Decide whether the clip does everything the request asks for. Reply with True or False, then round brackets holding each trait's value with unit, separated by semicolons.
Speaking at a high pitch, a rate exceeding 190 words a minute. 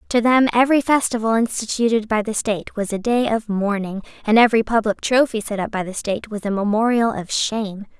True (220 Hz; 205 wpm)